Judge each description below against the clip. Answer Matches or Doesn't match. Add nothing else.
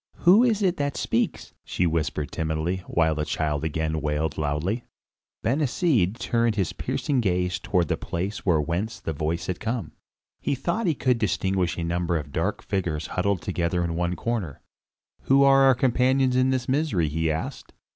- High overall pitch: Doesn't match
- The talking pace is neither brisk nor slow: Matches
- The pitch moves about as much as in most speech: Doesn't match